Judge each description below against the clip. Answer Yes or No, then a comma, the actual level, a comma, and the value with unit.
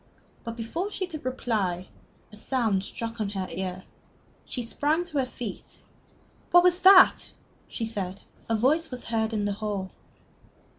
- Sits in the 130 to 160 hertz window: No, high, 230 Hz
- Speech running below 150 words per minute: No, average, 155 wpm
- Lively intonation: Yes, wide, 6.2 semitones